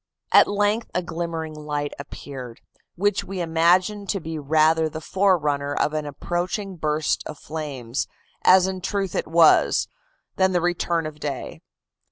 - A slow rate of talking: No, average, 150 wpm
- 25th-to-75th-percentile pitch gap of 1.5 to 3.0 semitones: No, average, 3.6 semitones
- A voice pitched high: No, medium, 165 Hz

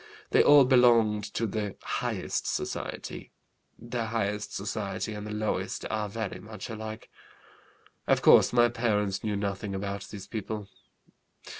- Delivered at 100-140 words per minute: Yes, slow, 135 wpm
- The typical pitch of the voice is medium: No, low, 105 Hz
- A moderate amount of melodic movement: No, narrow, 1.9 semitones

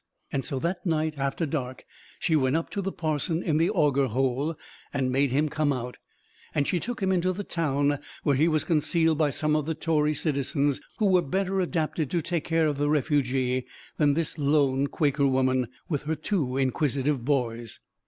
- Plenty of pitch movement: No, average, 3.2 semitones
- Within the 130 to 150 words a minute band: No, average, 195 wpm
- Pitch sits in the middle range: Yes, medium, 150 Hz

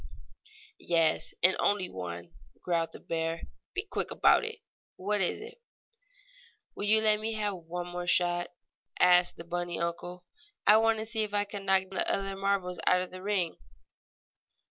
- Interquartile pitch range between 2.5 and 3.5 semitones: Yes, average, 2.8 semitones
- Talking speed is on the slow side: No, average, 165 wpm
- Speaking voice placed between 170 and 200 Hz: Yes, medium, 185 Hz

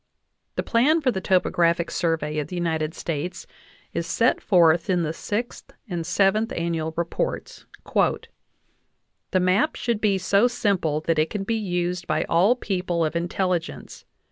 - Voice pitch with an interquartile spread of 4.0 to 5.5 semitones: No, average, 3.4 semitones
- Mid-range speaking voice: Yes, medium, 180 Hz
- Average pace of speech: Yes, average, 150 wpm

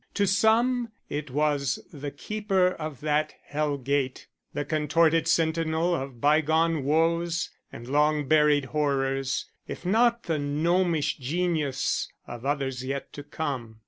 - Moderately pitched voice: Yes, medium, 150 Hz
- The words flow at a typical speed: No, slow, 130 wpm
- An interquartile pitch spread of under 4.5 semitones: Yes, average, 3.1 semitones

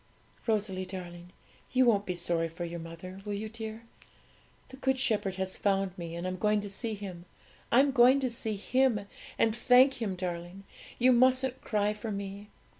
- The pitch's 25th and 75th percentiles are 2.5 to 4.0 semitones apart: No, average, 4.4 semitones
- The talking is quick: No, average, 180 wpm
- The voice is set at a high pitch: Yes, high, 205 Hz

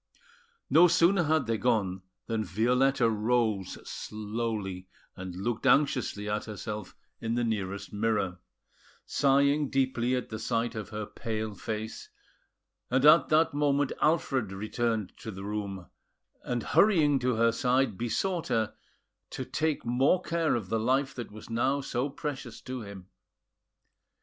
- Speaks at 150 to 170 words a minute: No, average, 140 wpm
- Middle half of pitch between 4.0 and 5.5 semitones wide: Yes, average, 4.3 semitones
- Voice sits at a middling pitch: No, low, 115 Hz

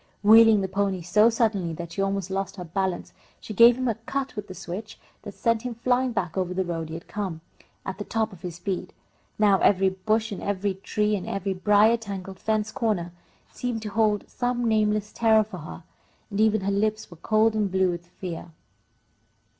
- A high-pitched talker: Yes, high, 205 Hz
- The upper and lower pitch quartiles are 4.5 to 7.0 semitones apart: No, average, 2.9 semitones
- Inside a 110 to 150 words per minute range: No, average, 200 wpm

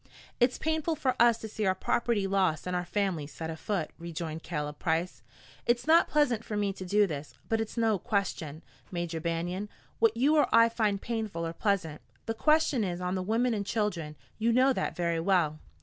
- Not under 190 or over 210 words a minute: Yes, average, 195 wpm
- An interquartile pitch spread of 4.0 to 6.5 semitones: Yes, average, 5.3 semitones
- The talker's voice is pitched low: No, high, 200 Hz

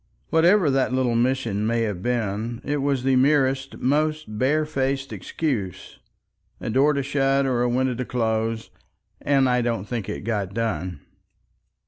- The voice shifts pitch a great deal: No, average, 3.3 semitones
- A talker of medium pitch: No, low, 125 Hz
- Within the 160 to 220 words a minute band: No, average, 150 wpm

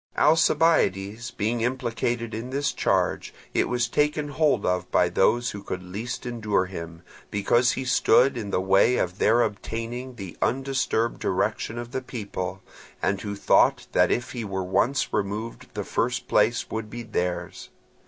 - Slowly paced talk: No, average, 160 wpm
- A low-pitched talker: Yes, low, 115 Hz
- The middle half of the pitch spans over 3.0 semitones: Yes, average, 4.0 semitones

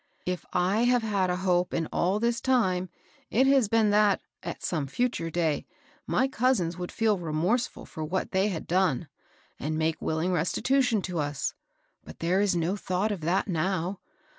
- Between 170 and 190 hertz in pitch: Yes, medium, 185 Hz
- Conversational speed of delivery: Yes, average, 180 wpm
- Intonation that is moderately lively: Yes, average, 4.4 semitones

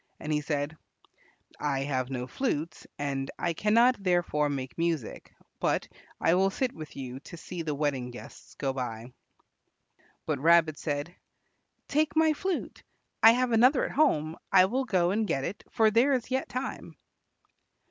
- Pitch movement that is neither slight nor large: No, wide, 8.2 semitones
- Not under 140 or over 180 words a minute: Yes, average, 160 wpm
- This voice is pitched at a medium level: Yes, medium, 165 Hz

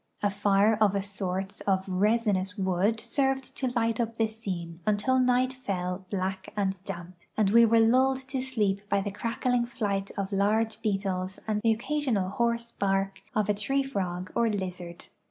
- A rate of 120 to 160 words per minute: No, average, 175 wpm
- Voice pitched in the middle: No, high, 205 Hz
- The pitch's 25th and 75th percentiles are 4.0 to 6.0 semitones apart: No, average, 3.3 semitones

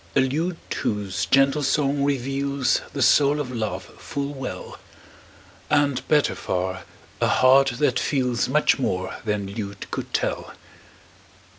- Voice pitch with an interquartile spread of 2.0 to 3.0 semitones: No, average, 3.9 semitones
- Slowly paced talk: Yes, slow, 130 wpm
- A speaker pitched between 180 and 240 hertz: No, low, 135 Hz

